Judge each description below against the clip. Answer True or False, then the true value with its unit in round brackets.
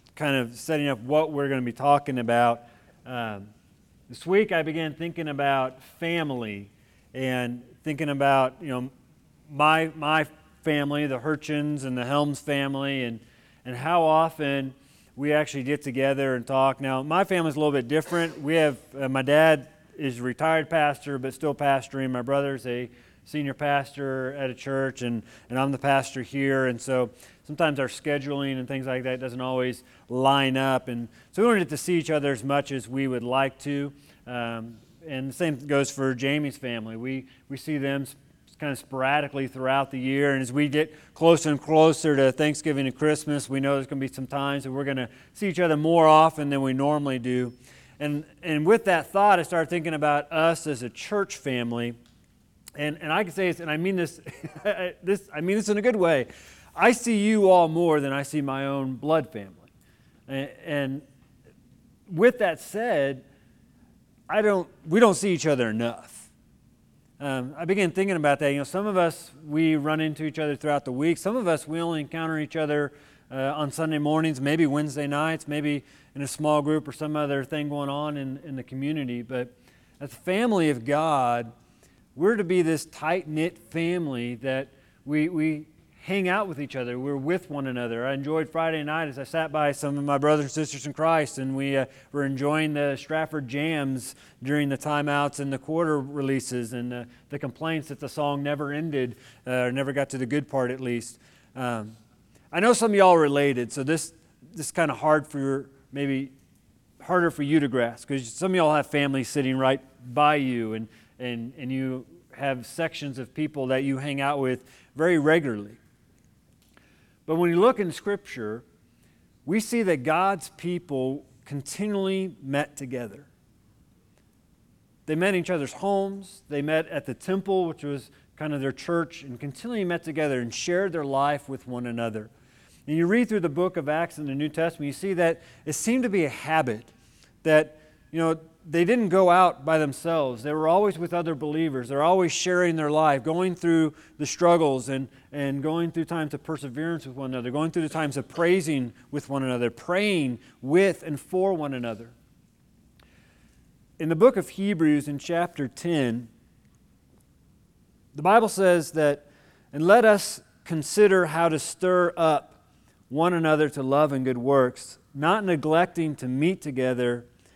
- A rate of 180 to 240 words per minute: True (190 wpm)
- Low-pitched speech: False (145 Hz)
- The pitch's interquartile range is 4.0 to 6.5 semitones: False (3.5 semitones)